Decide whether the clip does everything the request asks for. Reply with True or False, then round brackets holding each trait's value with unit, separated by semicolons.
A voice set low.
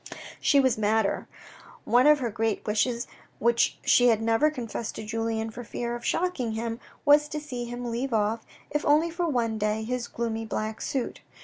False (235 Hz)